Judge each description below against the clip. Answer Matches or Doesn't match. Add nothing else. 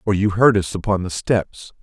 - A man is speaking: Matches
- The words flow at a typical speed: Doesn't match